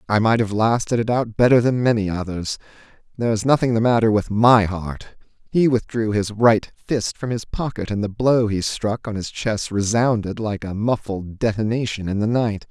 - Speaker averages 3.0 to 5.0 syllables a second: Yes, 4.9 syllables/s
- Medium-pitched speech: No, low, 110 Hz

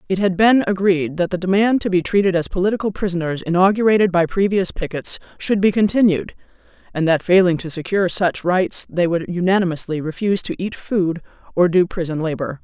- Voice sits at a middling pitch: Yes, medium, 180 Hz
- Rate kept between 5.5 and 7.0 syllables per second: Yes, 5.8 syllables/s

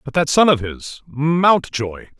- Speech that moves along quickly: No, slow, 135 wpm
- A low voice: No, medium, 145 Hz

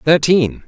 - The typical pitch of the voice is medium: Yes, medium, 155 Hz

